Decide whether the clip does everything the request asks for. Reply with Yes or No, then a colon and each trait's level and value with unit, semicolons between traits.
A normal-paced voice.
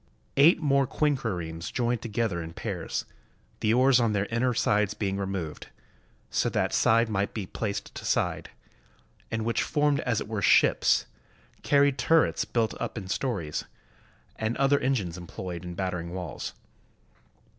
Yes: average, 150 wpm